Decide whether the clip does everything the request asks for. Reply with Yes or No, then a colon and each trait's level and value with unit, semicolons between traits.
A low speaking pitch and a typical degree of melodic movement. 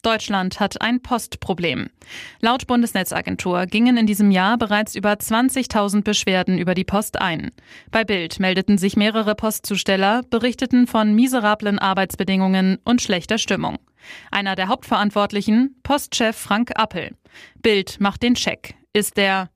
No: high, 210 Hz; average, 3.0 semitones